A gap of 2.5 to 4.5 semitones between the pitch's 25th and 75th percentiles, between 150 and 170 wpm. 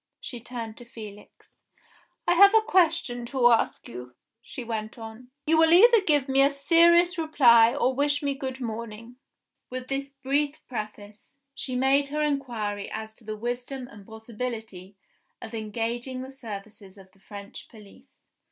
Yes: average, 4.2 semitones; average, 160 wpm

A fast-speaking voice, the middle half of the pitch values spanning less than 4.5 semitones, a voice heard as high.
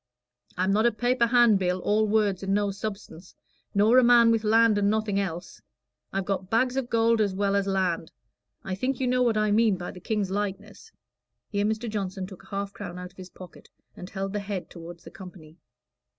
Yes: fast, 210 wpm; average, 2.7 semitones; high, 200 Hz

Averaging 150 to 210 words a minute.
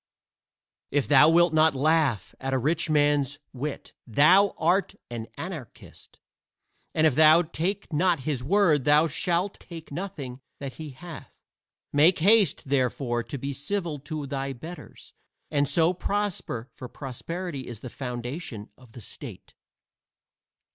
No: average, 140 wpm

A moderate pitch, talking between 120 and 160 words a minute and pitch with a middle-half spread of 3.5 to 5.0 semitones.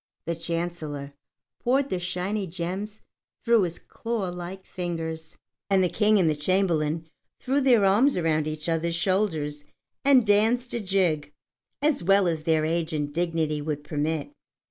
Yes: medium, 175 Hz; average, 150 wpm; average, 4.3 semitones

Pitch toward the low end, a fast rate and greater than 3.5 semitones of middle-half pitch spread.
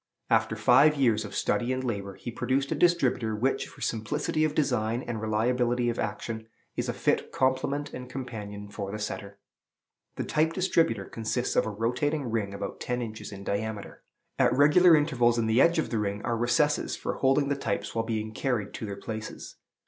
No: low, 120 Hz; average, 190 wpm; average, 3.9 semitones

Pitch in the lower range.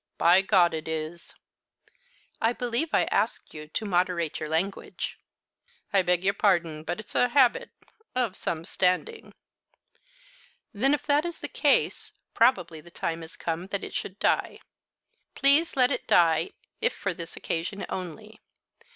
No: medium, 185 Hz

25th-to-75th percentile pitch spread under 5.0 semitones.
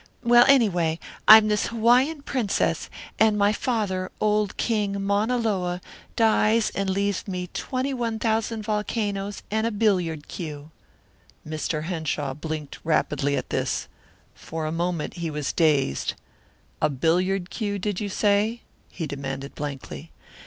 No: average, 5.3 semitones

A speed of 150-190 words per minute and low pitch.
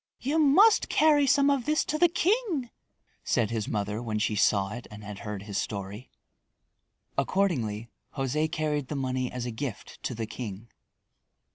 Yes: average, 165 wpm; low, 130 Hz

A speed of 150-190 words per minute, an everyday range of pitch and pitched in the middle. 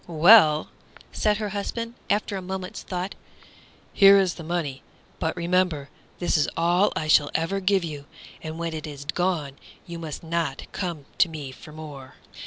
Yes: average, 170 wpm; average, 3.5 semitones; medium, 170 Hz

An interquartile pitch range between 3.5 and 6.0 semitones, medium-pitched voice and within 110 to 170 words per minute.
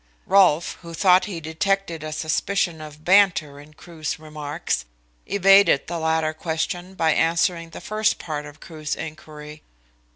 No: average, 2.8 semitones; medium, 160 Hz; average, 140 wpm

